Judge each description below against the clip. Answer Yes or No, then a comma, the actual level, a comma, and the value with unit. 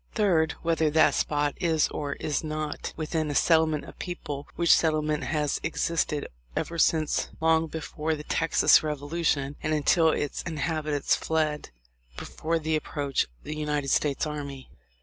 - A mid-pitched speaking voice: Yes, medium, 155 Hz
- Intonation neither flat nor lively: No, narrow, 1.5 semitones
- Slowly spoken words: No, average, 150 wpm